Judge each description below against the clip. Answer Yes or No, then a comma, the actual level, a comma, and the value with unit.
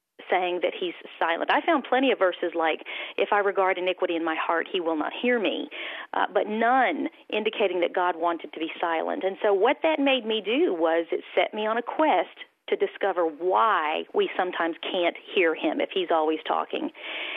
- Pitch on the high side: Yes, high, 210 Hz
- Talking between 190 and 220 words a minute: Yes, average, 200 wpm